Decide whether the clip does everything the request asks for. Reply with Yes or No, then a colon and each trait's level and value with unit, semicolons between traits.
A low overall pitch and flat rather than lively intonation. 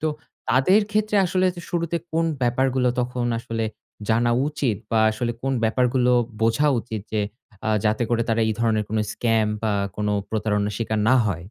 No: low, 120 Hz; average, 3.3 semitones